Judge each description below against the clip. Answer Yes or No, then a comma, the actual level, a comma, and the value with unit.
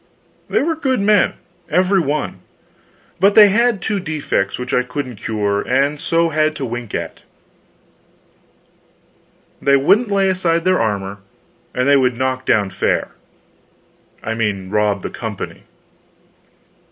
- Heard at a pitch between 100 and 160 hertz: Yes, medium, 140 Hz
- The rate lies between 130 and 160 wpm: Yes, slow, 135 wpm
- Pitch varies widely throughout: Yes, wide, 8.6 semitones